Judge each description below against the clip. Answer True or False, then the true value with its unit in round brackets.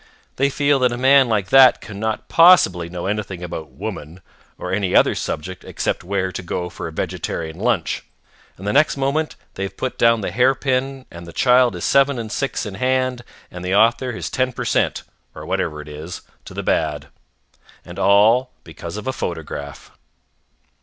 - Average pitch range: False (6.6 semitones)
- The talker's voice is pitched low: True (105 Hz)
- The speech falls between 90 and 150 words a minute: False (185 wpm)